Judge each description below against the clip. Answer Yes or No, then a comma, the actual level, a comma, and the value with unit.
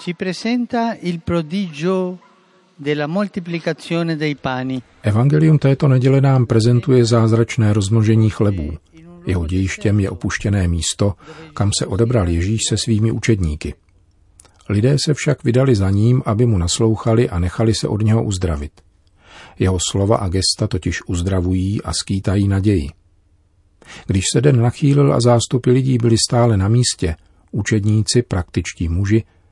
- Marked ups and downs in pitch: Yes, wide, 6.4 semitones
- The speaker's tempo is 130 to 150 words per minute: No, average, 120 wpm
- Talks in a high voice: No, low, 110 Hz